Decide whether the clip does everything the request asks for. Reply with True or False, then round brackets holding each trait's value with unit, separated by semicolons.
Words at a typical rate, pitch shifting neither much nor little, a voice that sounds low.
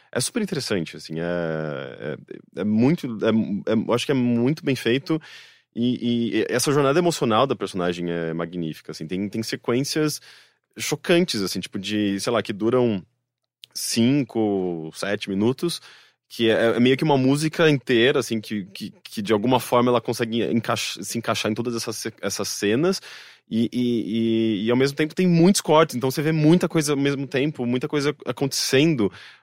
True (175 wpm; 4.2 semitones; 120 Hz)